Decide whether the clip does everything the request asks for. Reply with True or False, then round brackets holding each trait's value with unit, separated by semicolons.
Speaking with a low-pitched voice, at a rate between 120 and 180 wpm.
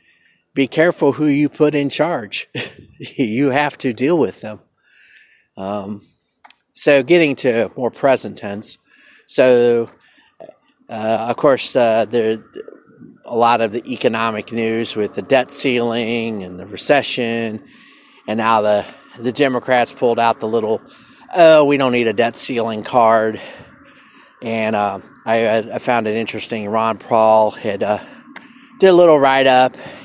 True (120 Hz; 145 wpm)